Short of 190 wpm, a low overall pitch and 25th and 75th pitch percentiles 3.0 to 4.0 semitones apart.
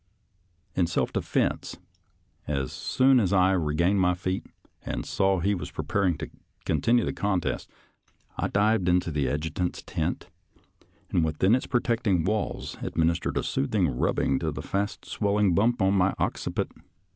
Yes: average, 155 wpm; very low, 95 Hz; average, 3.5 semitones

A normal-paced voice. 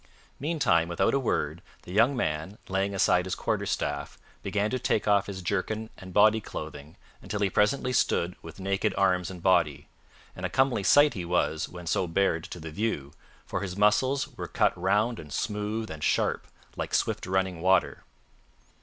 Yes: average, 175 wpm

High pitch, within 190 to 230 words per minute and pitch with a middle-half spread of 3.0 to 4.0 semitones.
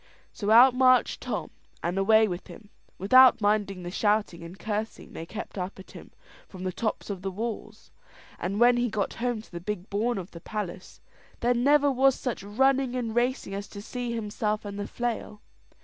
Yes: high, 215 Hz; average, 195 wpm; average, 3.6 semitones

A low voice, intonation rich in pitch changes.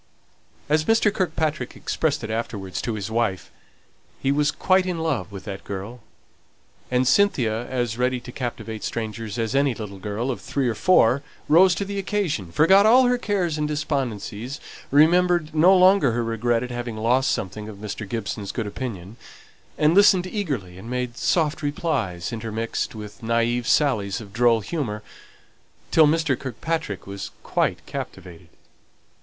Yes: low, 125 Hz; wide, 6.4 semitones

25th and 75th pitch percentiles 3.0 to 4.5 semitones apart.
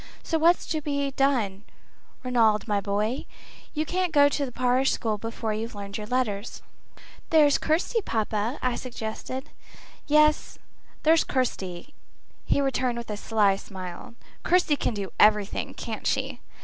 No: average, 5.3 semitones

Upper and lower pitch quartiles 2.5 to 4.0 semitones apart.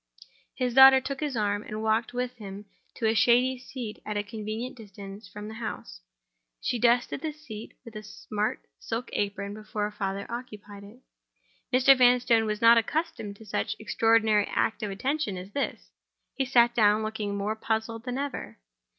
Yes: average, 3.1 semitones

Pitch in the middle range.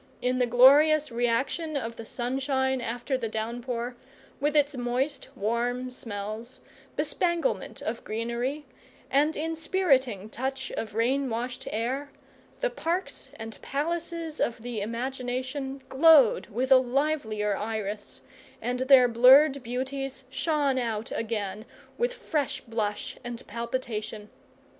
No: very high, 255 Hz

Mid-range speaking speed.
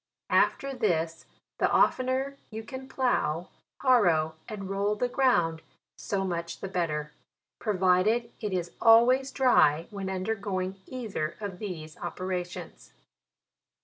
No: slow, 120 wpm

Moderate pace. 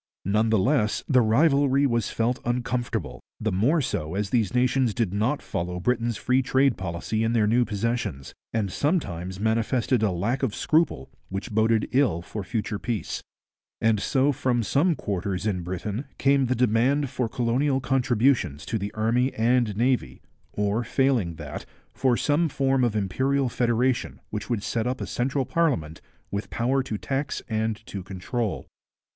Yes: average, 165 wpm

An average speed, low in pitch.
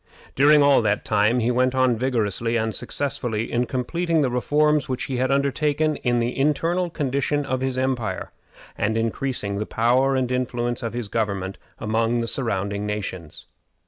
Yes: average, 160 wpm; low, 125 Hz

